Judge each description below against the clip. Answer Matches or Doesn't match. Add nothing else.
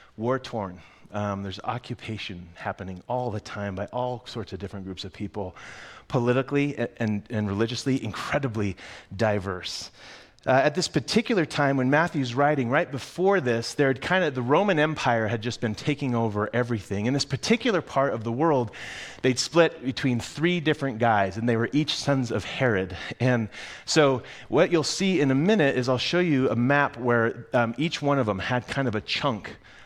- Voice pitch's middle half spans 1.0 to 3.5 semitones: Doesn't match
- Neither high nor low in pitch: Doesn't match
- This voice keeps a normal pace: Matches